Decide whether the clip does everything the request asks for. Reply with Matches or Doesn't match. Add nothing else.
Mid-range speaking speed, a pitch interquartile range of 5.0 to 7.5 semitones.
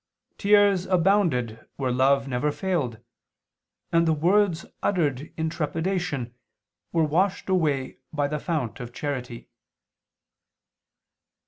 Doesn't match